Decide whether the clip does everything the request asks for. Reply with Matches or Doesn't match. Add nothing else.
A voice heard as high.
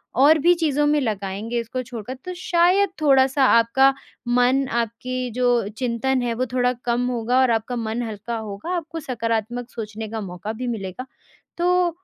Matches